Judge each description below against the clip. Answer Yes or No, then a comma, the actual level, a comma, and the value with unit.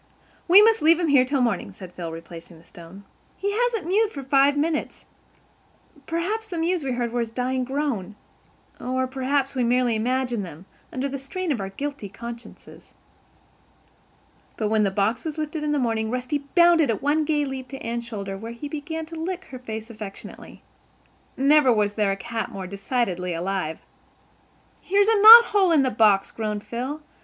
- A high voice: Yes, very high, 255 Hz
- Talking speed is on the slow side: No, average, 185 wpm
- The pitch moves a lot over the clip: Yes, wide, 6.2 semitones